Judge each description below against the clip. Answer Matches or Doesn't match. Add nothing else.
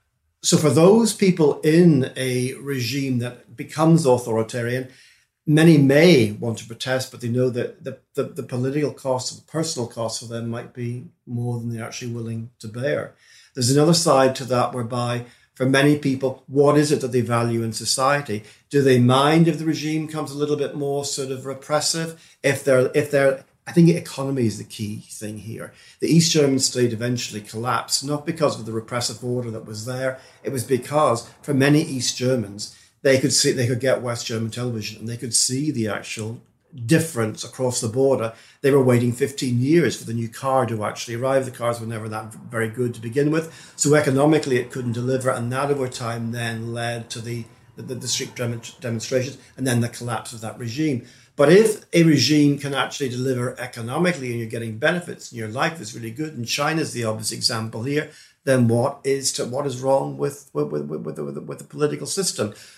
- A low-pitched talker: Matches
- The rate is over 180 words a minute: Matches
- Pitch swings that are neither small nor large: Matches